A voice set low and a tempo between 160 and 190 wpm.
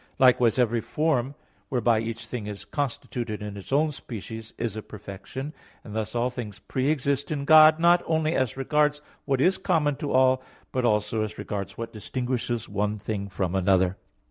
Yes: low, 120 Hz; average, 175 wpm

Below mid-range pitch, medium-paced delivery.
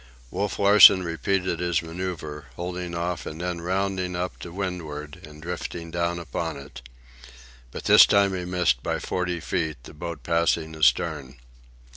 Yes: very low, 85 Hz; average, 150 wpm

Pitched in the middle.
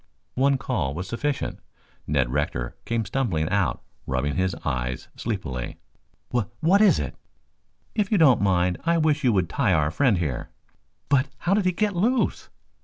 No: low, 110 Hz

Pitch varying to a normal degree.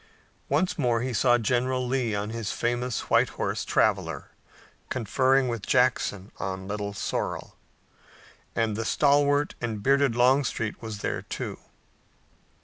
Yes: average, 3.3 semitones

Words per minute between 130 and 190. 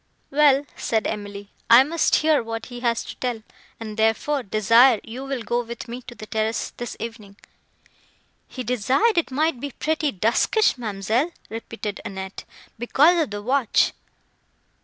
Yes: average, 155 wpm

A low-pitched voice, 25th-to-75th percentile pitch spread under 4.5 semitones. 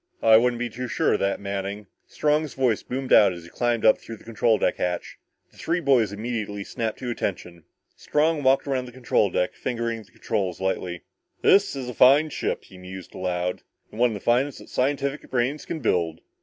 No: low, 115 Hz; average, 4.9 semitones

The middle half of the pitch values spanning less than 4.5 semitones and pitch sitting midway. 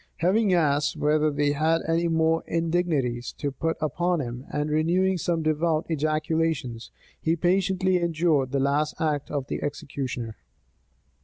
Yes: average, 2.8 semitones; medium, 155 Hz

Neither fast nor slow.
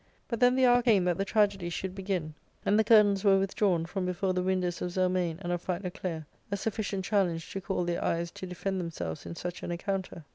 No: fast, 220 wpm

